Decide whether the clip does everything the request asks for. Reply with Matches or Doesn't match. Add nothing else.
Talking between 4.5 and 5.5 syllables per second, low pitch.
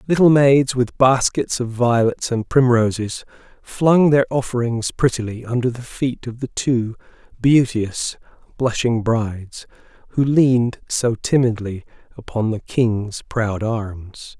Doesn't match